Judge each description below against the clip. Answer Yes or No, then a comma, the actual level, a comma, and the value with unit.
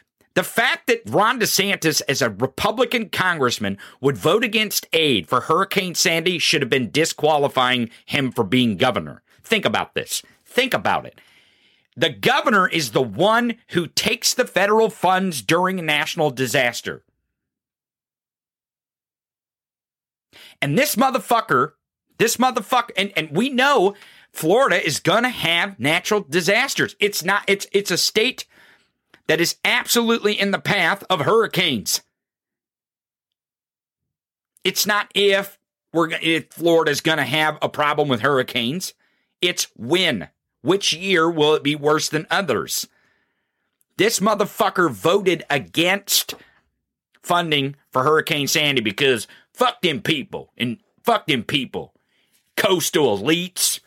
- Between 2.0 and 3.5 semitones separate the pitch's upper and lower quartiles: No, wide, 5.5 semitones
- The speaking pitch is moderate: Yes, medium, 175 Hz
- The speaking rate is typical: No, slow, 125 wpm